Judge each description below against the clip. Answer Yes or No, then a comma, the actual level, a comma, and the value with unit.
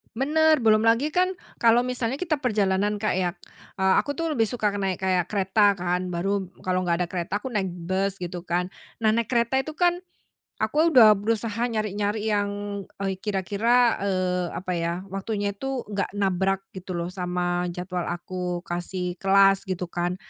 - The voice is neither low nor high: No, high, 195 Hz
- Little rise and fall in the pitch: No, average, 3.8 semitones